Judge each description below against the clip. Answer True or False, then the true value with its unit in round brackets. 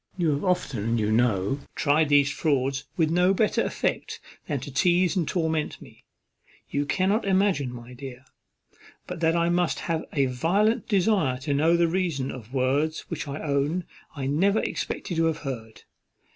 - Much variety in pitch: False (4.7 semitones)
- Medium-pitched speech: True (155 Hz)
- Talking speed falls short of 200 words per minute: True (170 wpm)